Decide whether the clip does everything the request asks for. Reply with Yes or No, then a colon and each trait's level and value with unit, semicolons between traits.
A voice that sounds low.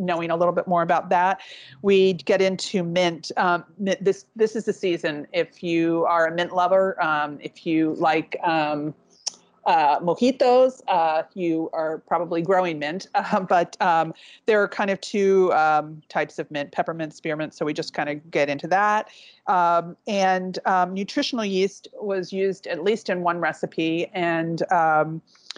No: medium, 175 Hz